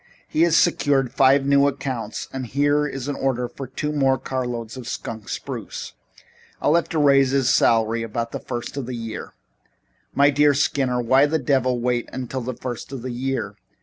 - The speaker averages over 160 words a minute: Yes, average, 185 wpm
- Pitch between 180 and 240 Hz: No, low, 130 Hz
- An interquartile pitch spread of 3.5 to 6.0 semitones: No, narrow, 2.6 semitones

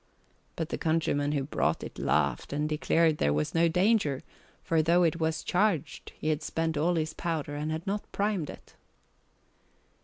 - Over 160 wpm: Yes, average, 175 wpm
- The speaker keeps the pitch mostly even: Yes, narrow, 2.1 semitones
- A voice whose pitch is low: No, medium, 160 Hz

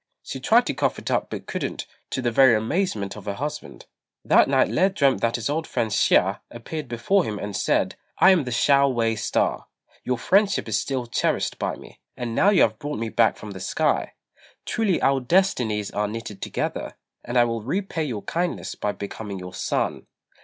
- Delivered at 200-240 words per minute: Yes, fast, 205 wpm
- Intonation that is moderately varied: No, wide, 5.7 semitones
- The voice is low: Yes, low, 120 Hz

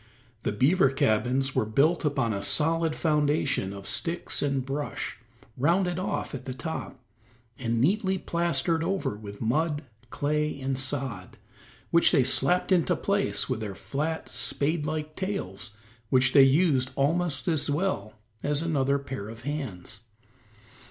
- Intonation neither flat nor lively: Yes, average, 4.2 semitones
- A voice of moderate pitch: Yes, medium, 145 Hz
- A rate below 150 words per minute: Yes, average, 140 wpm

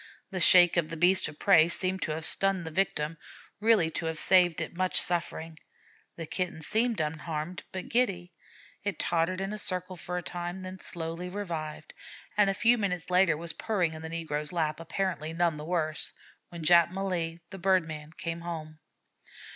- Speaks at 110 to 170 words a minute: No, average, 185 wpm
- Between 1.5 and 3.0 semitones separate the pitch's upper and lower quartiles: Yes, narrow, 2.6 semitones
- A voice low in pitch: No, medium, 175 Hz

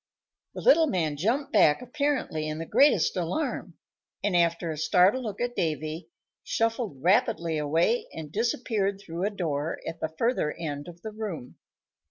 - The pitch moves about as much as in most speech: No, wide, 6.2 semitones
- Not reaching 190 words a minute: Yes, average, 160 wpm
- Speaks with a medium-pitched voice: Yes, medium, 180 Hz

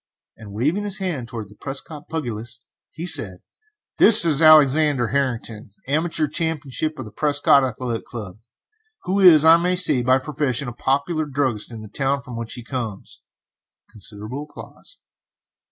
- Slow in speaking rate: No, average, 150 wpm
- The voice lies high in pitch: No, low, 135 Hz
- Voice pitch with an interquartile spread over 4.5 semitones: Yes, average, 5.0 semitones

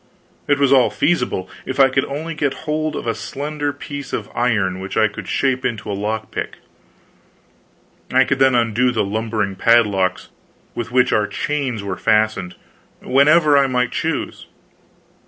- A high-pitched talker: No, low, 125 Hz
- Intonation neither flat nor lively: Yes, average, 4.5 semitones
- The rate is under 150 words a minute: No, average, 160 wpm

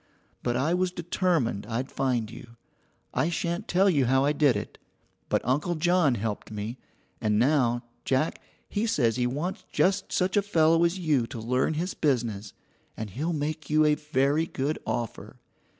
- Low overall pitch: No, medium, 145 Hz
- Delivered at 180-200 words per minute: No, average, 170 wpm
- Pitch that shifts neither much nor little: No, wide, 5.8 semitones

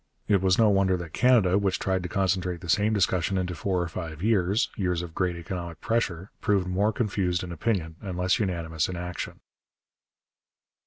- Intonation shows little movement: Yes, narrow, 2.2 semitones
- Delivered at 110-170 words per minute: No, average, 180 wpm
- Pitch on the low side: Yes, very low, 90 Hz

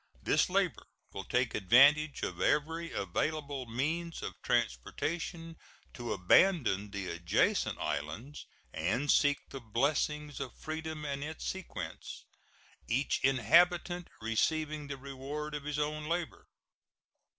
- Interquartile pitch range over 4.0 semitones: Yes, average, 4.7 semitones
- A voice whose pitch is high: No, medium, 145 Hz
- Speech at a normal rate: No, slow, 115 wpm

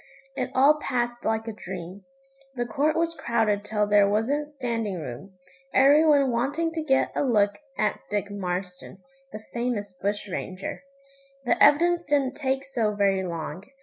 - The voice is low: No, high, 225 Hz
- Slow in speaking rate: No, average, 155 wpm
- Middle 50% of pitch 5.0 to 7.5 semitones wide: Yes, average, 5.3 semitones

